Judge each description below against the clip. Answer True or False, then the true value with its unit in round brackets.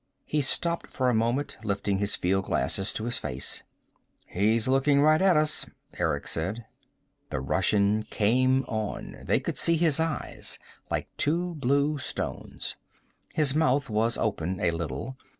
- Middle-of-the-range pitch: False (120 Hz)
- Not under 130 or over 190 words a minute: True (145 wpm)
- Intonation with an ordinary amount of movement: False (6.5 semitones)